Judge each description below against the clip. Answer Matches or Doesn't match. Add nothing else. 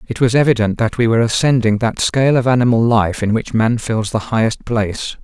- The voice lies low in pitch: Matches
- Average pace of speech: Doesn't match